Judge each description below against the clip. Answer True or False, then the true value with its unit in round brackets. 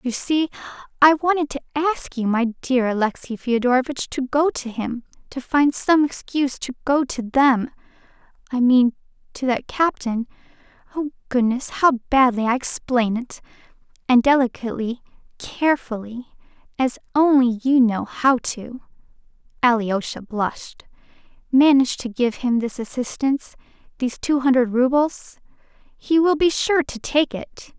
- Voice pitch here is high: True (260 Hz)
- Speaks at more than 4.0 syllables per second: True (4.5 syllables/s)